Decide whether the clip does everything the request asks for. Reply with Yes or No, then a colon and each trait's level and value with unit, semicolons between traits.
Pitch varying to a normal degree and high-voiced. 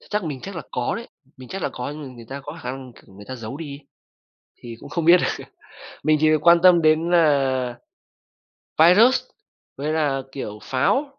No: average, 4.7 semitones; medium, 150 Hz